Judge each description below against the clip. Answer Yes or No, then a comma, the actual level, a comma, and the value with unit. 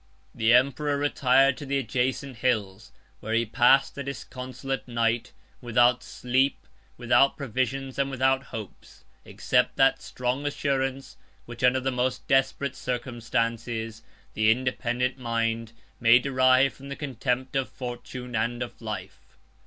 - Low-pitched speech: Yes, low, 125 Hz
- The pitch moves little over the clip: Yes, narrow, 2.3 semitones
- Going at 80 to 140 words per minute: Yes, slow, 135 wpm